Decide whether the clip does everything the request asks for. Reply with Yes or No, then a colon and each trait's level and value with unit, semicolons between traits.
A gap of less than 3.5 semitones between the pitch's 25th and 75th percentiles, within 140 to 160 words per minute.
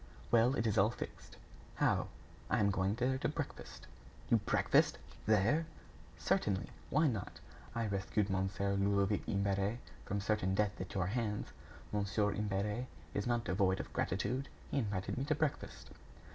Yes: average, 3.0 semitones; average, 150 wpm